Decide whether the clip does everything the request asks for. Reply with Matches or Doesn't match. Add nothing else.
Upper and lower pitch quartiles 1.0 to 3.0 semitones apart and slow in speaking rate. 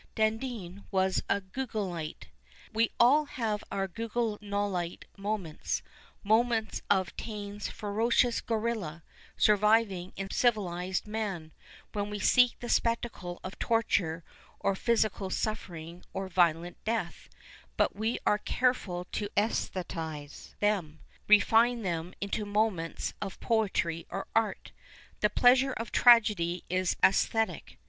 Doesn't match